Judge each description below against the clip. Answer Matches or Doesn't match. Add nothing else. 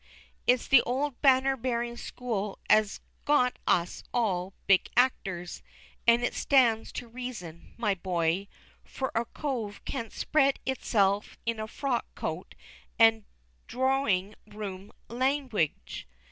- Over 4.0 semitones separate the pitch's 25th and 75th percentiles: Matches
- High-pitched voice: Matches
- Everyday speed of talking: Doesn't match